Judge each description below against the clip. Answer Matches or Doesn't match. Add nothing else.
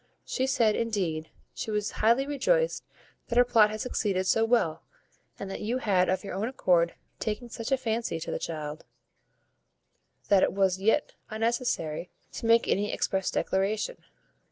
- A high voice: Matches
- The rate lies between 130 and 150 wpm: Doesn't match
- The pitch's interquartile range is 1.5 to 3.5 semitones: Doesn't match